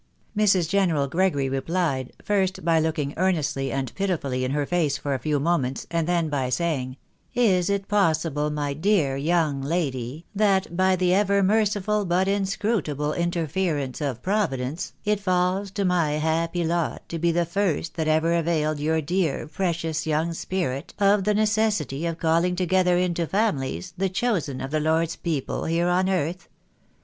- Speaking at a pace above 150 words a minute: Yes, average, 165 wpm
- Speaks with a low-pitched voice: No, medium, 170 Hz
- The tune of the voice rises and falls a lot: No, average, 4.0 semitones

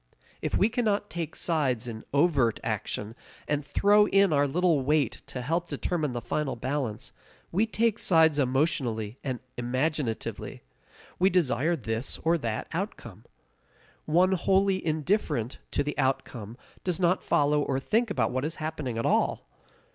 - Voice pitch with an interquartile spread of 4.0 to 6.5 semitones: Yes, wide, 5.5 semitones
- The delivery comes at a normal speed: Yes, average, 145 wpm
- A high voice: No, medium, 150 Hz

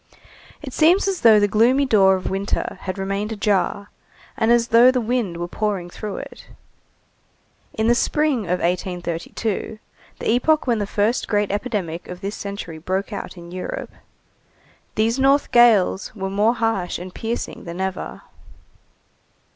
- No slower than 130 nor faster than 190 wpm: Yes, average, 155 wpm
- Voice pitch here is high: Yes, high, 205 Hz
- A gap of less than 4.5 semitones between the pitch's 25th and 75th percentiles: Yes, average, 3.8 semitones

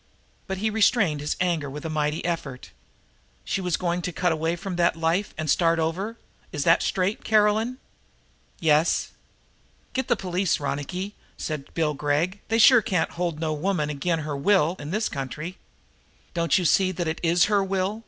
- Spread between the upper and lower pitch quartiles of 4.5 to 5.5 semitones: No, average, 3.9 semitones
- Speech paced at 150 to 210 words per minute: Yes, average, 175 wpm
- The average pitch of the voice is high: No, medium, 175 Hz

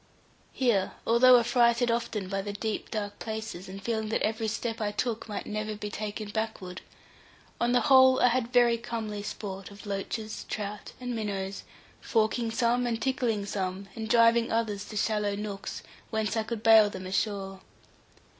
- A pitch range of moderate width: No, narrow, 2.3 semitones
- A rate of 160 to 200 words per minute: Yes, average, 165 wpm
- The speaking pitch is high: Yes, high, 220 Hz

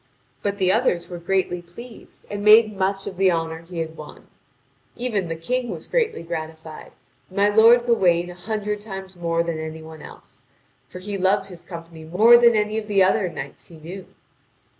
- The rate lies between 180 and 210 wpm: Yes, average, 190 wpm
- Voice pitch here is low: No, high, 190 Hz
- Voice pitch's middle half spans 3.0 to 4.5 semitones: Yes, average, 3.8 semitones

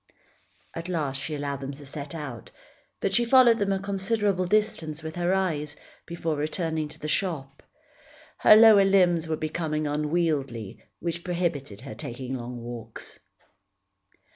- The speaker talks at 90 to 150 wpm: Yes, average, 145 wpm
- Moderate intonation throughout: Yes, average, 4.5 semitones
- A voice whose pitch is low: No, medium, 160 Hz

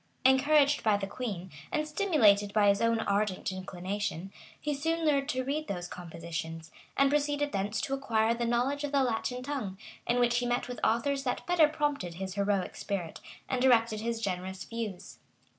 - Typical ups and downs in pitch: No, wide, 5.8 semitones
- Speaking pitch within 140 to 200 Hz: No, high, 230 Hz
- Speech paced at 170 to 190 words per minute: Yes, average, 180 wpm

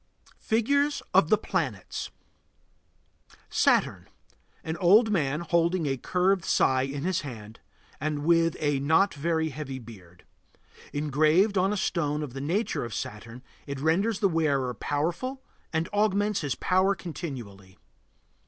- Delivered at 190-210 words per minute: No, slow, 135 wpm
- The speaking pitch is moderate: Yes, medium, 160 Hz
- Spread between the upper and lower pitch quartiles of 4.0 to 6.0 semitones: Yes, wide, 5.6 semitones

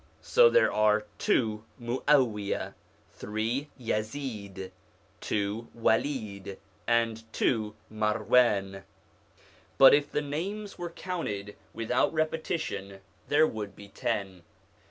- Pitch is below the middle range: Yes, low, 115 Hz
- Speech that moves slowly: Yes, slow, 95 wpm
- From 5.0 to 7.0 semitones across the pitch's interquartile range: Yes, wide, 5.6 semitones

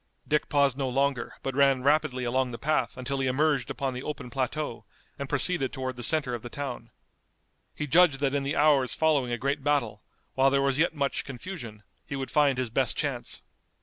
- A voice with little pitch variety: Yes, narrow, 2.3 semitones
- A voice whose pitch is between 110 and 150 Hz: Yes, low, 135 Hz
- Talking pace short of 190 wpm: No, fast, 205 wpm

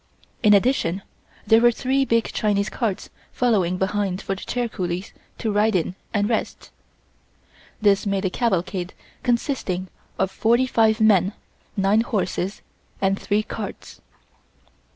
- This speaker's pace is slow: Yes, slow, 130 wpm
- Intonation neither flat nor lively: Yes, average, 3.2 semitones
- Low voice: No, high, 205 Hz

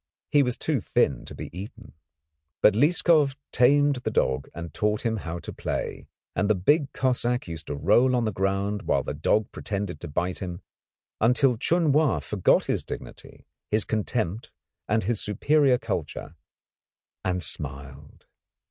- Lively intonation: Yes, wide, 6.1 semitones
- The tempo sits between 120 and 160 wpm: Yes, average, 155 wpm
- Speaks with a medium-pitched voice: No, low, 105 Hz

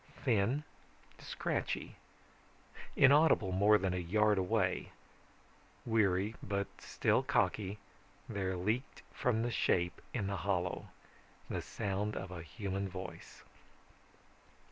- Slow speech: Yes, slow, 105 wpm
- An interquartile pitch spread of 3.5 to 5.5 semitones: No, average, 2.7 semitones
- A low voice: Yes, low, 100 Hz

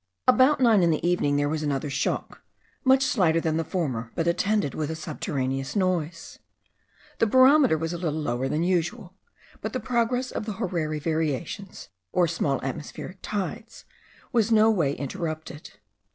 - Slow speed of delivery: No, average, 160 wpm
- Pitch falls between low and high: Yes, medium, 170 Hz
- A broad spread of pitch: Yes, wide, 5.9 semitones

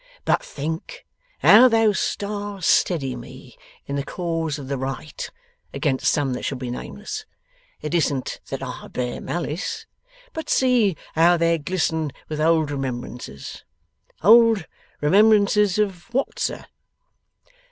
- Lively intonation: Yes, wide, 6.7 semitones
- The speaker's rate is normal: No, slow, 130 wpm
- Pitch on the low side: No, medium, 165 Hz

